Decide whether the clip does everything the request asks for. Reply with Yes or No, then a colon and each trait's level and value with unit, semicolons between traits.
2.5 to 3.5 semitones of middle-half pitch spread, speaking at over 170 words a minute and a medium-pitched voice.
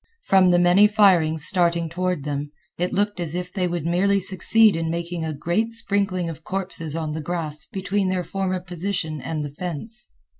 Yes: average, 3.0 semitones; average, 185 wpm; medium, 175 Hz